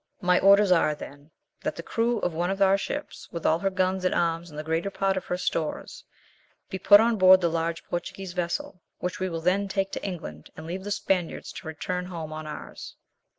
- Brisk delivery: Yes, fast, 220 wpm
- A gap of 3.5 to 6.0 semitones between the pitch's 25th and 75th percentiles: No, average, 2.8 semitones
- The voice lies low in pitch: No, medium, 180 Hz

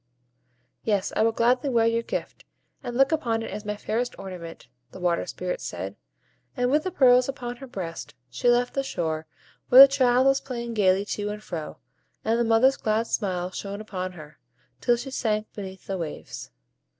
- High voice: Yes, high, 225 Hz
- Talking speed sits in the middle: Yes, average, 185 wpm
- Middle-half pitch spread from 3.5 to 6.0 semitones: Yes, average, 4.6 semitones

